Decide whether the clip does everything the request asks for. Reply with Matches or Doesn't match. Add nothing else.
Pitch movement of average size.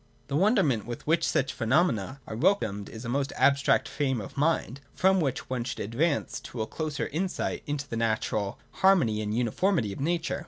Doesn't match